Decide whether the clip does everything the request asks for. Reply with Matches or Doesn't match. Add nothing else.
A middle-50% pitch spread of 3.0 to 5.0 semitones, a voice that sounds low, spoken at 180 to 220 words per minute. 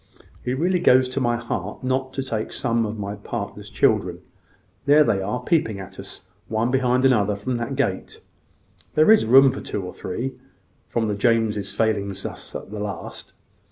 Matches